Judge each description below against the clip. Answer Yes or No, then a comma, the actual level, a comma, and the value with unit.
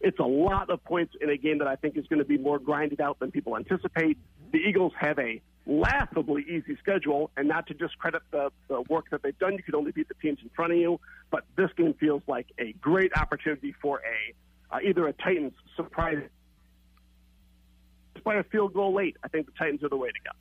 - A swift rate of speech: Yes, fast, 225 wpm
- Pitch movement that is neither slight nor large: Yes, average, 3.5 semitones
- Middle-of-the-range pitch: Yes, medium, 150 Hz